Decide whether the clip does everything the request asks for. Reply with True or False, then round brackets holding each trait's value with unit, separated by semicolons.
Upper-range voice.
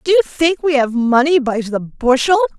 True (285 Hz)